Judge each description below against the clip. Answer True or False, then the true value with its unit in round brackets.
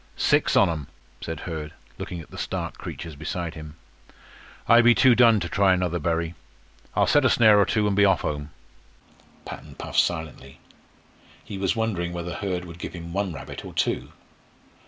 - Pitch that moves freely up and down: False (3.8 semitones)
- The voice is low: True (85 Hz)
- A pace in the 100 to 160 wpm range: False (180 wpm)